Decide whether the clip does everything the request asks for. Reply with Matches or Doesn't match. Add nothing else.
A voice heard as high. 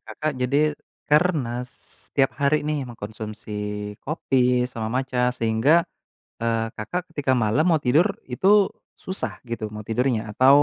Doesn't match